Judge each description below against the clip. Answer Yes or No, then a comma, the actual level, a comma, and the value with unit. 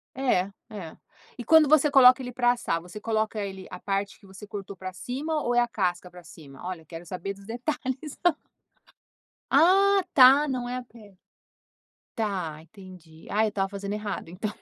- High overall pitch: Yes, high, 210 Hz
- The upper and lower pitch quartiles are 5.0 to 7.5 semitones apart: Yes, average, 5.3 semitones